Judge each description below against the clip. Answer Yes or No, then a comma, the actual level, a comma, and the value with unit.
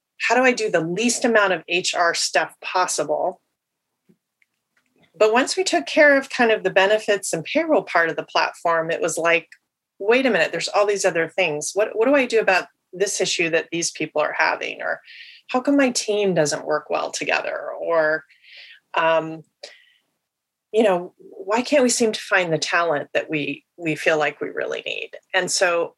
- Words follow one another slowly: No, average, 190 wpm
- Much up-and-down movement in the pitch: Yes, wide, 7.5 semitones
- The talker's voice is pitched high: Yes, high, 200 Hz